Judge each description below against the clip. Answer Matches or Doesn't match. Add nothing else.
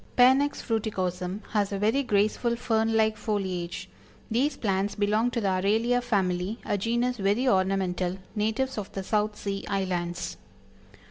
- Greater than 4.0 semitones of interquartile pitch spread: Doesn't match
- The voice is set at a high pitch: Matches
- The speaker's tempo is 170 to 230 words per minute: Doesn't match